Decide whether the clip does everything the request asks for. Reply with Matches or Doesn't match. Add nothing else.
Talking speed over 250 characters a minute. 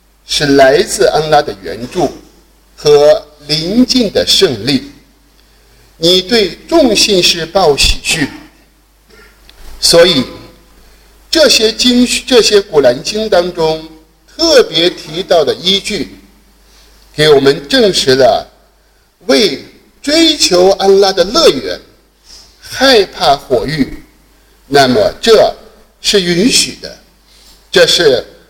Doesn't match